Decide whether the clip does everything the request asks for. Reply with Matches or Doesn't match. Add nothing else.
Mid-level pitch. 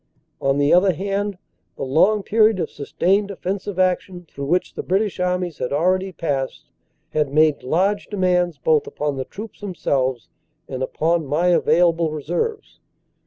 Matches